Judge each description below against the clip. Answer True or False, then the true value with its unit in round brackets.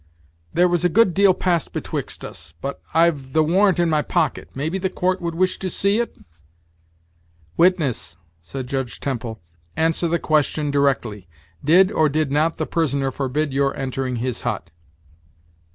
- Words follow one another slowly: False (160 wpm)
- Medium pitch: True (155 Hz)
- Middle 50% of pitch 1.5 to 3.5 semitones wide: False (4.6 semitones)